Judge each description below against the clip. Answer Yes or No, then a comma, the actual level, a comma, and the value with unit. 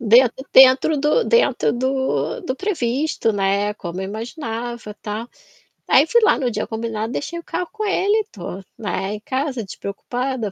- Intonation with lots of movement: Yes, wide, 5.7 semitones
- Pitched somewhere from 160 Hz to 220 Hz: No, high, 245 Hz